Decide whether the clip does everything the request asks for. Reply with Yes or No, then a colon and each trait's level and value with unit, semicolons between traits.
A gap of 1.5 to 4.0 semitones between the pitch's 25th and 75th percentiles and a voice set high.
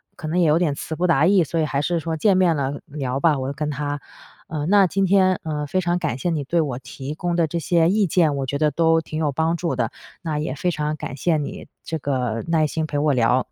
No: average, 3.2 semitones; medium, 155 Hz